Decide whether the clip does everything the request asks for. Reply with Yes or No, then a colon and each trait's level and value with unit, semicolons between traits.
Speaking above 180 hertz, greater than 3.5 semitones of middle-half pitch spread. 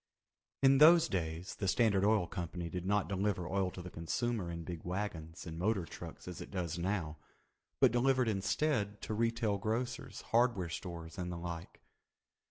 No: very low, 95 Hz; average, 4.3 semitones